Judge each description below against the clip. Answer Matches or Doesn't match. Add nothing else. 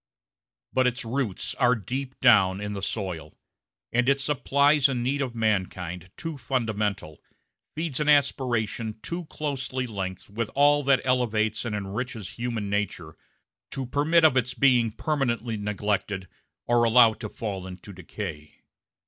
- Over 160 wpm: Doesn't match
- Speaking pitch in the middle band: Doesn't match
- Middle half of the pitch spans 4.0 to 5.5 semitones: Matches